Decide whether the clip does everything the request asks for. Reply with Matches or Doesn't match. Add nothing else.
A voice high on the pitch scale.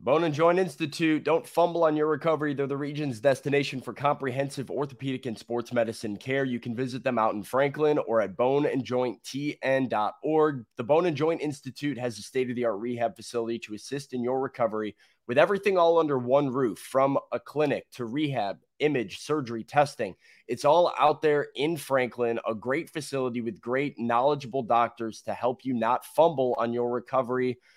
Doesn't match